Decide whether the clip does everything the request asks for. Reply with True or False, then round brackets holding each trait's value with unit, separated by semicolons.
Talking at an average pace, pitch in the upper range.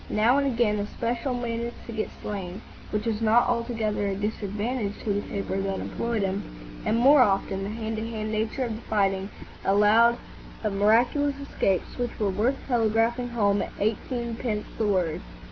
True (165 wpm; 220 Hz)